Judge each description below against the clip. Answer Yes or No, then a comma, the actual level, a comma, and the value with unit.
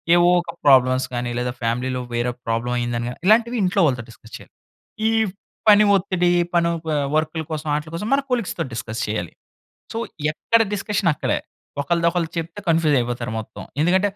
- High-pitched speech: No, medium, 155 Hz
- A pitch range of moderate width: No, wide, 6.8 semitones